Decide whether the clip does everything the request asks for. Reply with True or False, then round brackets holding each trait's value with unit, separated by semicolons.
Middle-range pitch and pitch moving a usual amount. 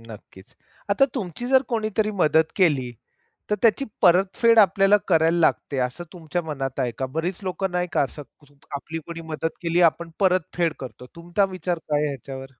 True (170 Hz; 4.5 semitones)